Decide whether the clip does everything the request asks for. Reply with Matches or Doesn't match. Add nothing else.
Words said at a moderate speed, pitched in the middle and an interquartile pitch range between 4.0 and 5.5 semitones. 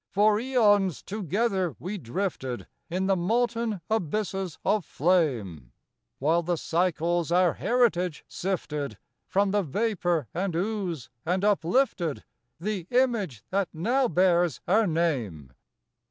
Doesn't match